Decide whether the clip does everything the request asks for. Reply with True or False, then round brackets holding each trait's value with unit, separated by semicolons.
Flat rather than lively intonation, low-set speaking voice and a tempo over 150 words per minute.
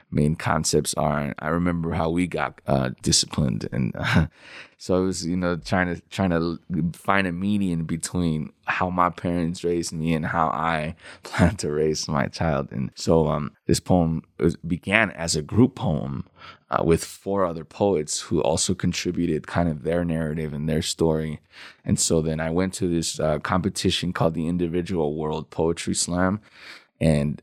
True (2.2 semitones; 85 Hz; 175 wpm)